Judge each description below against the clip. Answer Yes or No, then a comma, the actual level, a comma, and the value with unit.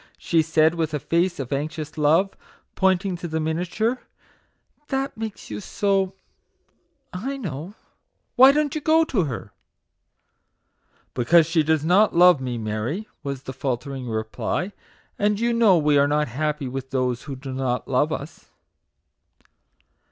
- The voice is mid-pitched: Yes, medium, 160 Hz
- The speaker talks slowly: No, average, 155 wpm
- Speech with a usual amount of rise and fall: No, wide, 6.1 semitones